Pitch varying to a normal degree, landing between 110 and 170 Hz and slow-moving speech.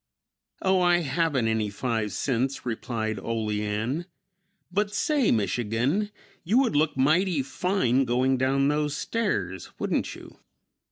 No: wide, 7.7 semitones; low, 135 Hz; slow, 120 wpm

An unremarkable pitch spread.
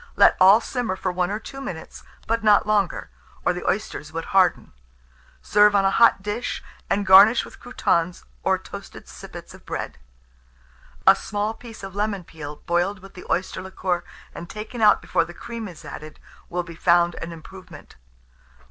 Yes: average, 3.4 semitones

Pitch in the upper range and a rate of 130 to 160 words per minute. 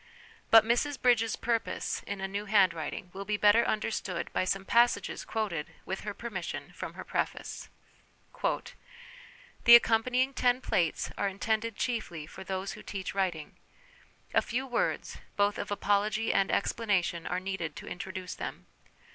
Yes: high, 205 Hz; average, 155 wpm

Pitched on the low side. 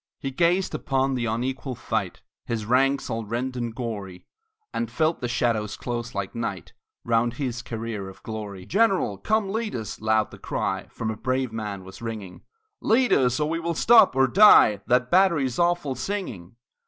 Yes: low, 125 Hz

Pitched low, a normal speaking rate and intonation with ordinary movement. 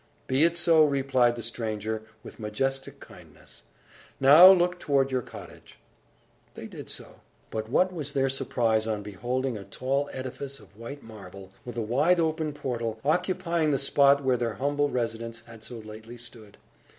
Yes: low, 130 Hz; average, 165 wpm; average, 4.1 semitones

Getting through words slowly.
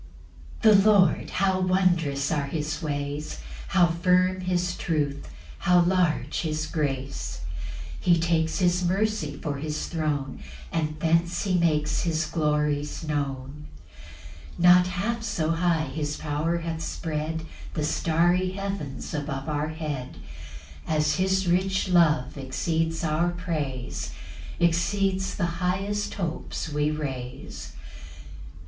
Yes: slow, 120 wpm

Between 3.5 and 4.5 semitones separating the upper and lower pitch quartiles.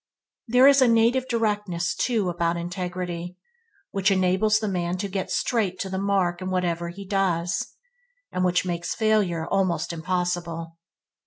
No: average, 3.0 semitones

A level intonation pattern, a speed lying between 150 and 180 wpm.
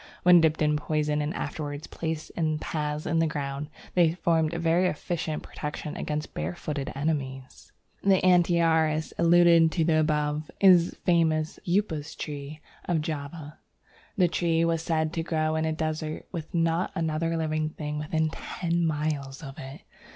Yes: narrow, 1.8 semitones; average, 155 wpm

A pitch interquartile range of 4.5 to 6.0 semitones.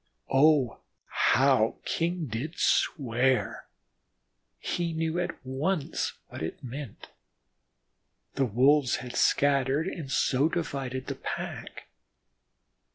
No: average, 3.8 semitones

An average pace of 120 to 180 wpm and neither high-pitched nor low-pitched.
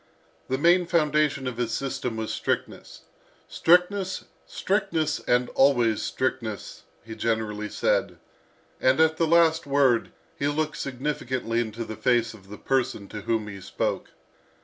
No: average, 140 wpm; low, 130 Hz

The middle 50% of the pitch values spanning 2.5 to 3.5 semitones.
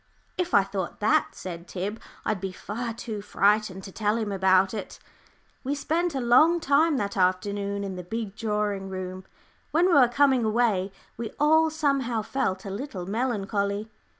No: average, 4.8 semitones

